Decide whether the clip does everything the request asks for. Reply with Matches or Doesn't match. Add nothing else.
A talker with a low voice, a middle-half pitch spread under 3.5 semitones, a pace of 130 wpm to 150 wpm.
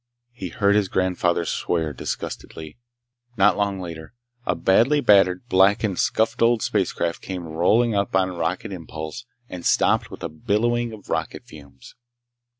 Doesn't match